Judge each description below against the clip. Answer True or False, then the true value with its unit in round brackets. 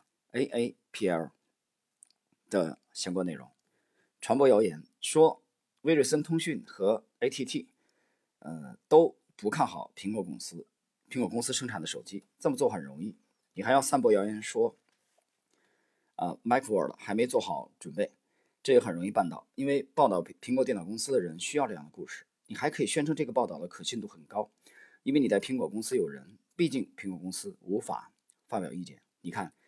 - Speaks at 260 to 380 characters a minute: True (275 characters per minute)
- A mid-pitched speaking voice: True (160 Hz)